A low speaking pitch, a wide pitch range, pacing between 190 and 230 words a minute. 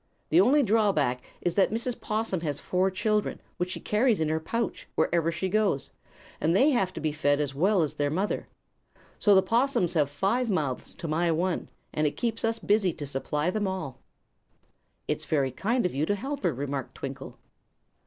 No: medium, 180 Hz; wide, 5.9 semitones; average, 195 wpm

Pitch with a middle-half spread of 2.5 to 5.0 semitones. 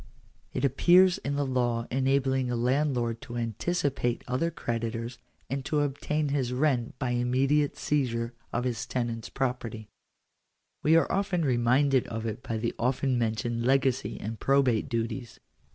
Yes: average, 2.9 semitones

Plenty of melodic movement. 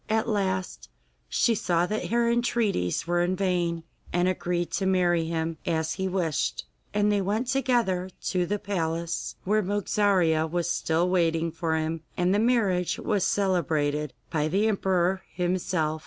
No: average, 3.5 semitones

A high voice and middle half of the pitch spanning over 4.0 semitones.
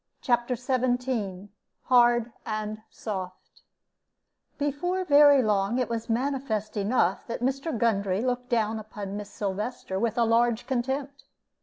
No: high, 235 Hz; average, 3.5 semitones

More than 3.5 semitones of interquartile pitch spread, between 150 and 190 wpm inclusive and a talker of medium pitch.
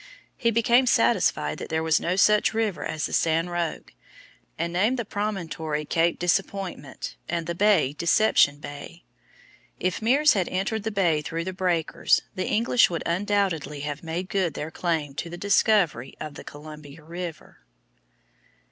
Yes: average, 4.2 semitones; average, 155 wpm; medium, 175 Hz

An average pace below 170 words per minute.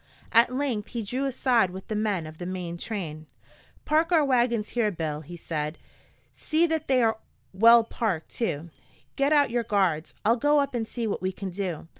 No: average, 195 wpm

